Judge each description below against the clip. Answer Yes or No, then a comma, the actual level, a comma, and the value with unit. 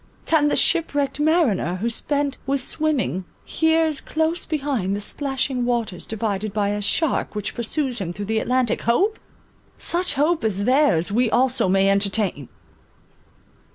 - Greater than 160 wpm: No, average, 150 wpm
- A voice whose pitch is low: No, high, 245 Hz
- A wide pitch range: Yes, wide, 6.4 semitones